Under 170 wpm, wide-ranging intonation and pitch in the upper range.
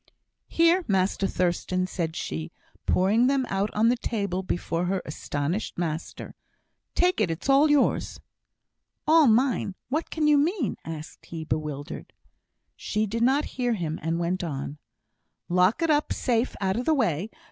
Yes: average, 155 wpm; wide, 7.6 semitones; high, 195 Hz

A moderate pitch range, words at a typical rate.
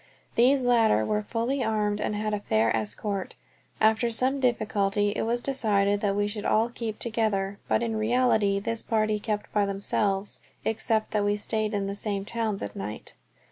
No: narrow, 2.2 semitones; average, 180 wpm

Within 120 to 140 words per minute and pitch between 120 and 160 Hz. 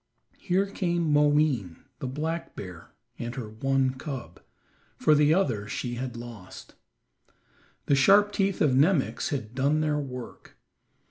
Yes: slow, 135 wpm; low, 135 Hz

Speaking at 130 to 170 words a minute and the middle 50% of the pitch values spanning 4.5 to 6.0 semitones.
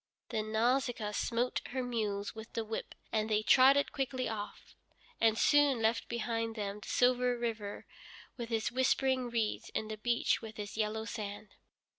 No: average, 160 wpm; narrow, 2.4 semitones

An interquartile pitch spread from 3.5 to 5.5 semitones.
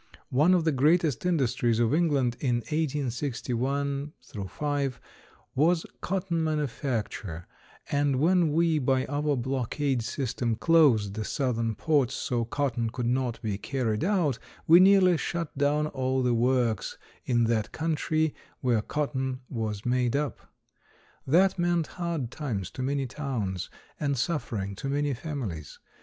Yes: average, 4.3 semitones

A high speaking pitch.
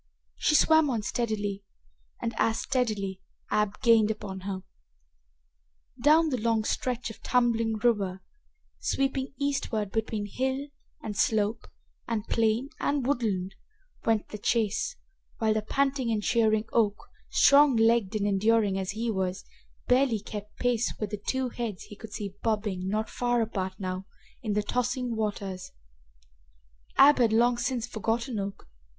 Yes: high, 225 Hz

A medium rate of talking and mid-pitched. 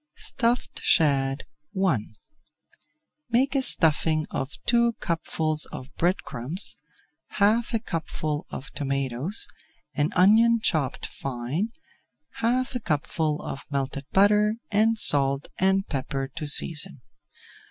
No: slow, 110 wpm; medium, 160 Hz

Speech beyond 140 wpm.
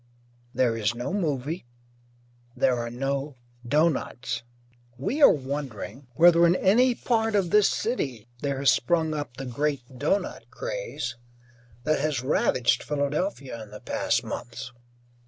No: slow, 135 wpm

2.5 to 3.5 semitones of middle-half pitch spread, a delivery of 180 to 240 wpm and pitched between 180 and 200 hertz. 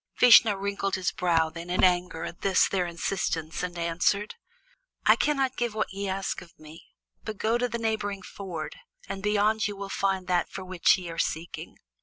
Yes: average, 3.1 semitones; average, 190 wpm; high, 190 Hz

